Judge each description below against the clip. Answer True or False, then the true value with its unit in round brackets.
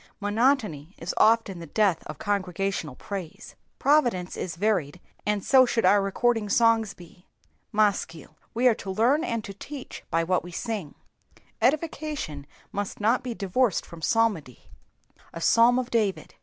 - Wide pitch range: False (4.7 semitones)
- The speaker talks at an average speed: True (150 wpm)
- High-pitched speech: True (205 Hz)